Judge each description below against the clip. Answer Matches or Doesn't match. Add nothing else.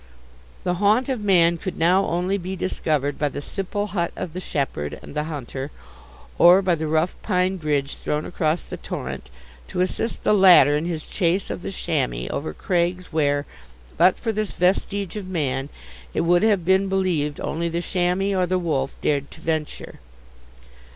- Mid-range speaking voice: Matches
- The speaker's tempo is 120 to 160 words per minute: Doesn't match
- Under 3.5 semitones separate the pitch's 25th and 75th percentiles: Doesn't match